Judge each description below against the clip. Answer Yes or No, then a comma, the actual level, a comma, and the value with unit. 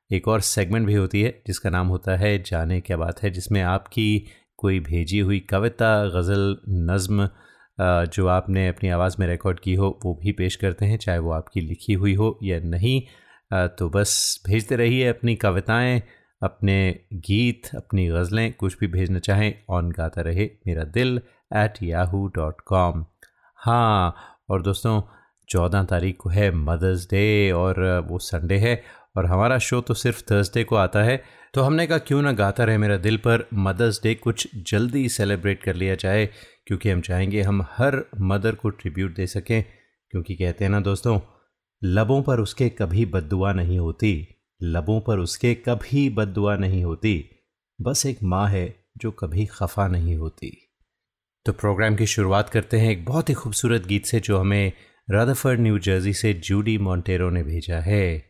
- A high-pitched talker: No, low, 100 Hz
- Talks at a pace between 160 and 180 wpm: Yes, average, 170 wpm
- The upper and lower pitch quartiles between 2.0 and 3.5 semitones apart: Yes, average, 3.1 semitones